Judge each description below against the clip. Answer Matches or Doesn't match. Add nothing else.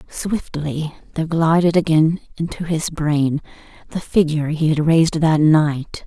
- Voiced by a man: Doesn't match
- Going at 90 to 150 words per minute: Matches